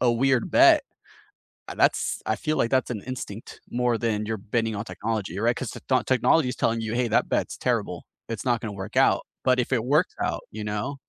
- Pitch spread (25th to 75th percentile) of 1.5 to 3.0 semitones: Yes, average, 2.7 semitones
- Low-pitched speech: Yes, low, 115 Hz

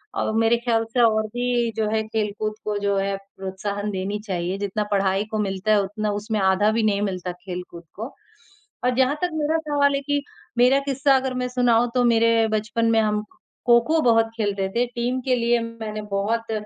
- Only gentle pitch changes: No, average, 3.1 semitones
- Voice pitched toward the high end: Yes, high, 220 Hz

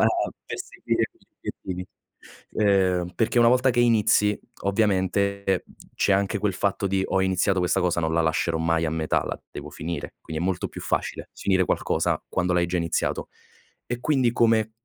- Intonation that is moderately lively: Yes, average, 3.2 semitones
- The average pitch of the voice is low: Yes, very low, 95 Hz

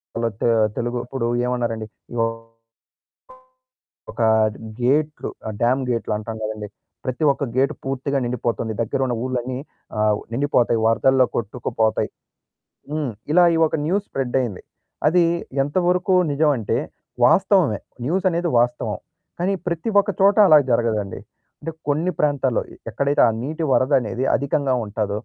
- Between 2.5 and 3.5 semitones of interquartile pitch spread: No, average, 4.5 semitones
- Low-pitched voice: Yes, low, 130 Hz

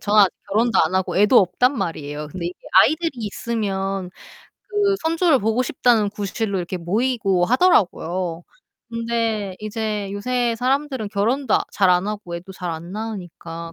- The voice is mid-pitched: No, high, 205 Hz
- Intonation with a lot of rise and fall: No, average, 4.4 semitones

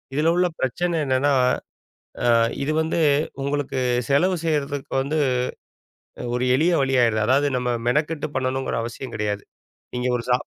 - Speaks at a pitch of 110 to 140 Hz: Yes, low, 135 Hz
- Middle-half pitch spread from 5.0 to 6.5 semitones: No, average, 3.6 semitones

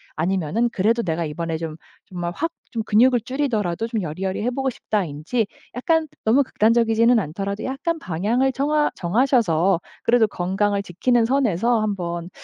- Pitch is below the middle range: No, high, 215 Hz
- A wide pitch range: Yes, wide, 5.7 semitones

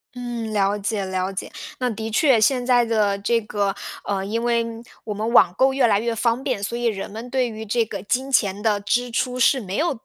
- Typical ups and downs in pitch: Yes, average, 3.2 semitones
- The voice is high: Yes, high, 225 Hz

